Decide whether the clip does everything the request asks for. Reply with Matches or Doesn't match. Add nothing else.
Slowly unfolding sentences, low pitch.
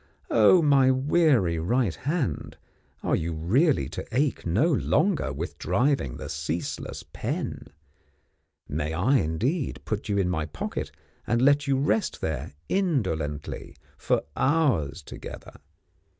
Matches